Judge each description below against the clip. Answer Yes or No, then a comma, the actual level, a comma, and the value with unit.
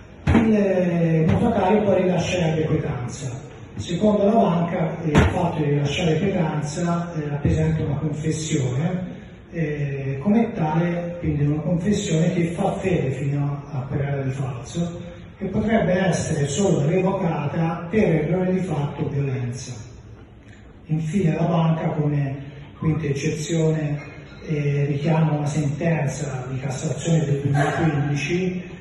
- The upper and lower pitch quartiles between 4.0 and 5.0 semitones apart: No, average, 3.3 semitones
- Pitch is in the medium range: Yes, medium, 155 Hz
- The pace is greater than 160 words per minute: No, slow, 115 wpm